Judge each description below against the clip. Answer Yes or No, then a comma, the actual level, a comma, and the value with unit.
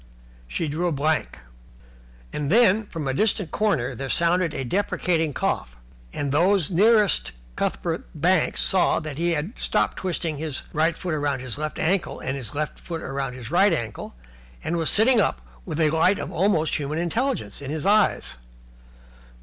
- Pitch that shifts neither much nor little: Yes, average, 4.5 semitones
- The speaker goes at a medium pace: Yes, average, 165 wpm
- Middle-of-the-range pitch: Yes, medium, 160 Hz